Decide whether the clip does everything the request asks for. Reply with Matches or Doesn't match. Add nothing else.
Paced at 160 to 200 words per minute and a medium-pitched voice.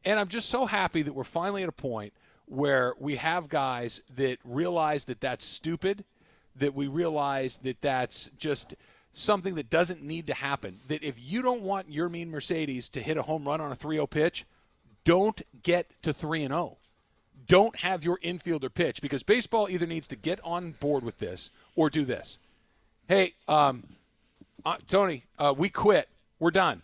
Matches